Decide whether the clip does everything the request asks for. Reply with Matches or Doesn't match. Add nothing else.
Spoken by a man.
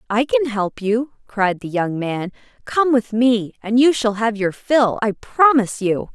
Doesn't match